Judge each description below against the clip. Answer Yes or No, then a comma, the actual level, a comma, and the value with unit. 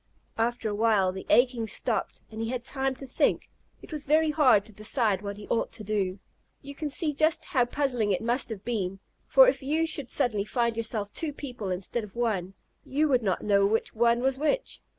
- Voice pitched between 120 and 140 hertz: No, high, 235 Hz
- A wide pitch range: No, average, 4.7 semitones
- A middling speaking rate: No, fast, 210 wpm